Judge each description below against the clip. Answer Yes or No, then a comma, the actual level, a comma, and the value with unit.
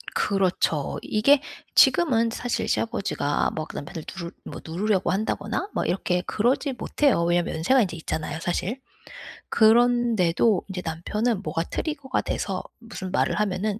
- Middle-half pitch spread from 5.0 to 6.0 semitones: Yes, average, 5.3 semitones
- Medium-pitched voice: No, high, 200 Hz